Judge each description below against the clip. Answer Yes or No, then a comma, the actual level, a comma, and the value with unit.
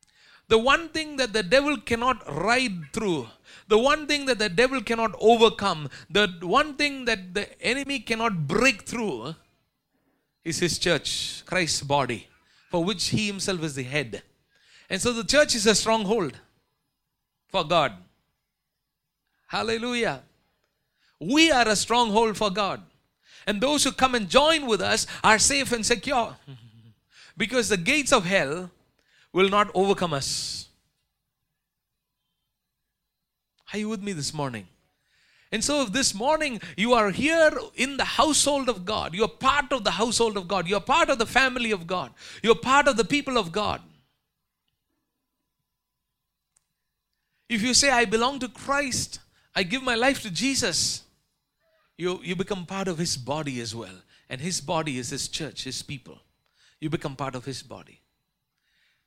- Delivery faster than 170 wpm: No, average, 155 wpm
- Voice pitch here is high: Yes, high, 215 Hz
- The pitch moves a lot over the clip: Yes, wide, 6.6 semitones